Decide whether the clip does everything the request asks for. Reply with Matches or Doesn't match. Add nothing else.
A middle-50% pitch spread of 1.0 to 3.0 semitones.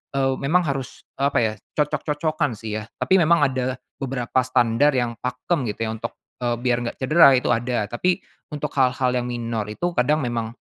Doesn't match